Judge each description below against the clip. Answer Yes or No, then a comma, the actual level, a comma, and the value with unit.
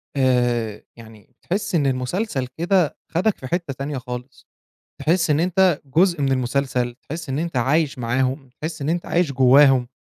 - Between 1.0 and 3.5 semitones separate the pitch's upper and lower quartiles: No, average, 4.8 semitones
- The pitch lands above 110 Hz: Yes, medium, 140 Hz